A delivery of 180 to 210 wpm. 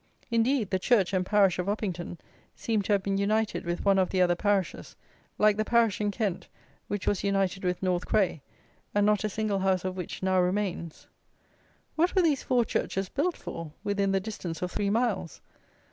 Yes: average, 190 wpm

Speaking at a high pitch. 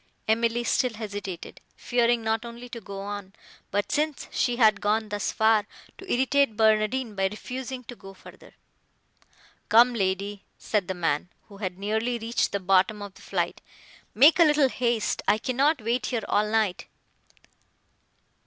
Yes: high, 220 Hz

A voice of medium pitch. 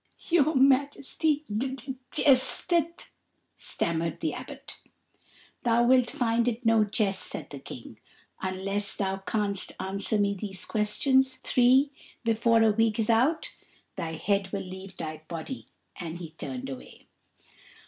No: high, 220 Hz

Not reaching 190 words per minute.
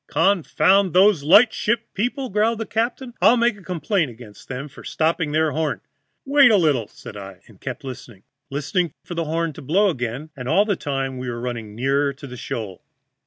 No: average, 195 wpm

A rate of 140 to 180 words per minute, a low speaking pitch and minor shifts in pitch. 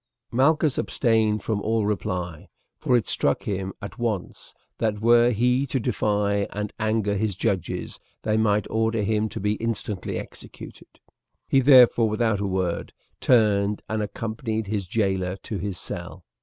Yes: average, 150 wpm; low, 110 Hz; narrow, 2.3 semitones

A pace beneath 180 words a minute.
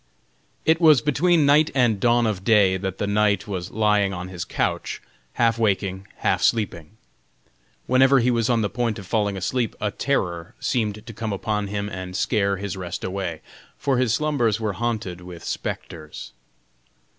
Yes: average, 170 wpm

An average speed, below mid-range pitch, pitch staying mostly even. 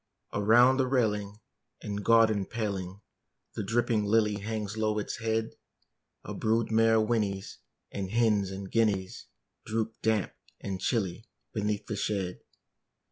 No: slow, 130 wpm; low, 105 Hz; narrow, 2.0 semitones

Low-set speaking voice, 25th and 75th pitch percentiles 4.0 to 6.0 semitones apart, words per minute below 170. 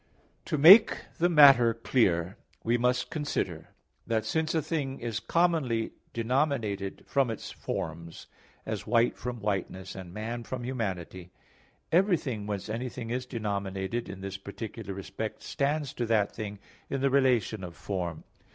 Yes: low, 115 Hz; average, 5.2 semitones; average, 140 wpm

